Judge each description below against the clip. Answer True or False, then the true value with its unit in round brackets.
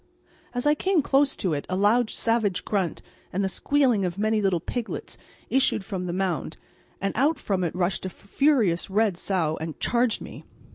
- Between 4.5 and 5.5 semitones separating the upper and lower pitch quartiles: True (5.1 semitones)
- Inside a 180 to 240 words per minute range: True (185 wpm)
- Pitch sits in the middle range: False (200 Hz)